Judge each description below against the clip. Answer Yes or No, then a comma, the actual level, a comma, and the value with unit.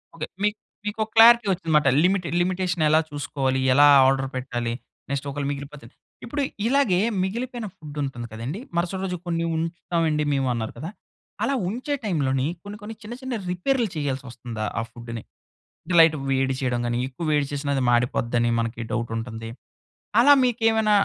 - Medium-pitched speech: Yes, medium, 150 Hz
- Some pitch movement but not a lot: No, wide, 7.5 semitones